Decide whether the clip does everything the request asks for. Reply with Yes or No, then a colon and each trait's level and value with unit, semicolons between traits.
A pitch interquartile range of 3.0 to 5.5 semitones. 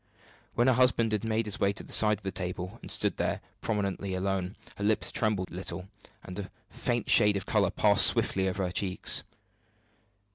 No: narrow, 2.5 semitones